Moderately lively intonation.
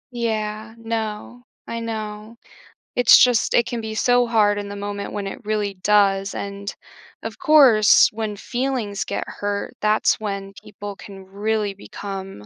No: narrow, 2.1 semitones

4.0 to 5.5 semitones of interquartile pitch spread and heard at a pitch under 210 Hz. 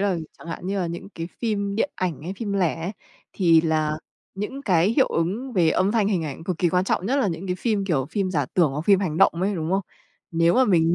No: average, 3.5 semitones; medium, 185 Hz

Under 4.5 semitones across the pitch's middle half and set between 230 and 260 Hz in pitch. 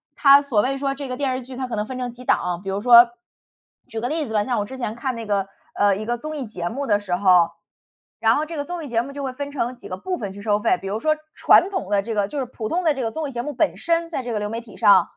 No: average, 5.2 semitones; high, 240 Hz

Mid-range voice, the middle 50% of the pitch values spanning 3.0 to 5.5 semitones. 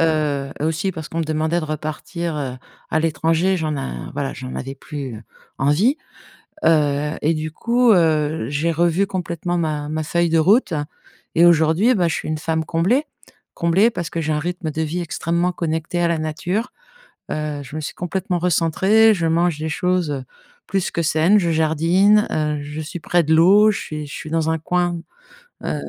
No: medium, 160 Hz; narrow, 2.5 semitones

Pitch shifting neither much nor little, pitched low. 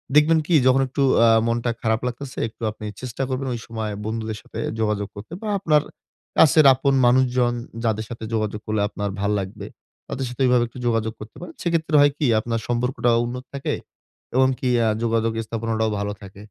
Yes: average, 3.1 semitones; low, 120 Hz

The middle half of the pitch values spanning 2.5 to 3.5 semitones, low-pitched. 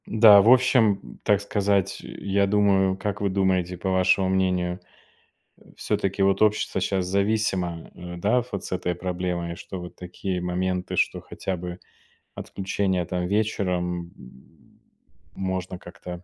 No: narrow, 1.9 semitones; very low, 95 Hz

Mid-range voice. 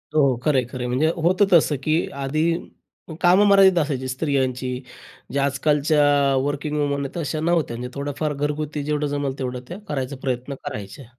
Yes: medium, 145 Hz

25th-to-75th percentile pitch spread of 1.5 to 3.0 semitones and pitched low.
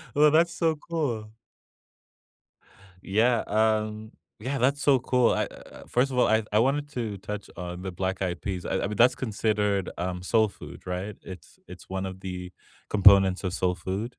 No: average, 4.8 semitones; low, 105 Hz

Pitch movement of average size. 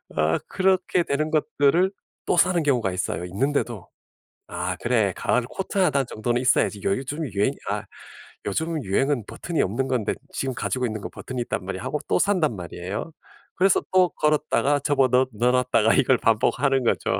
No: wide, 5.8 semitones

